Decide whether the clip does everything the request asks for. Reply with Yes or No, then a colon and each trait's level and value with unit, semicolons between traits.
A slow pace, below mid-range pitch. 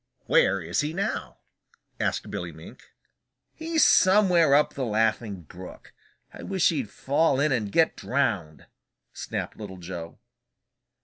Yes: slow, 130 wpm; low, 130 Hz